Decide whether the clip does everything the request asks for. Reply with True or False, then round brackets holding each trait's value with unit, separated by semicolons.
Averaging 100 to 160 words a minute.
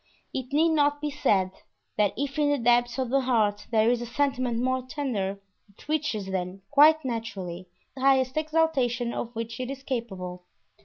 False (175 wpm)